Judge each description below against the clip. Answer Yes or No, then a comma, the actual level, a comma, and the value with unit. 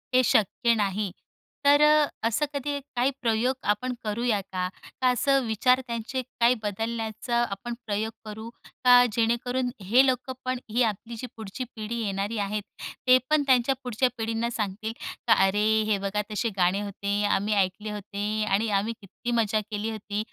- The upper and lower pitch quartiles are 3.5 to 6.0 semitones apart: No, average, 3.1 semitones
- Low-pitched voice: No, high, 225 Hz